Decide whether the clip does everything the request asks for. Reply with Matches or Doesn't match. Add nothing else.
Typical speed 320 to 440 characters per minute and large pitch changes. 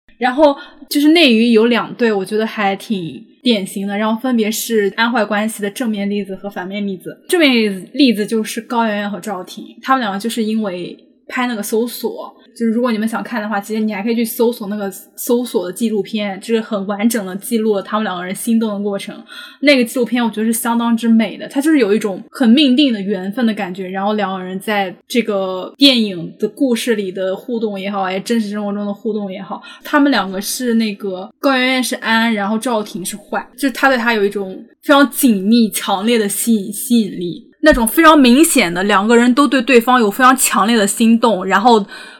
Doesn't match